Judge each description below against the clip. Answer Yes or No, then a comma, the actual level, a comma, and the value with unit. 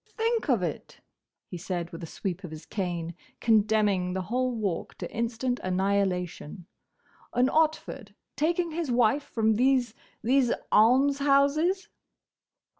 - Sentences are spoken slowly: Yes, slow, 115 wpm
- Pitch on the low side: No, high, 225 Hz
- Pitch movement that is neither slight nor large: No, wide, 6.8 semitones